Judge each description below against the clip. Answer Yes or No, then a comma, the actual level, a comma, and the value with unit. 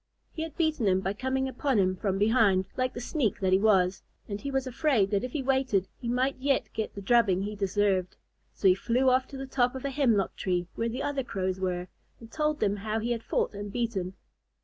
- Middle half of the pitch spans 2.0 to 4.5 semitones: No, average, 5.2 semitones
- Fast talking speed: Yes, fast, 235 wpm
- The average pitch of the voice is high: Yes, high, 225 Hz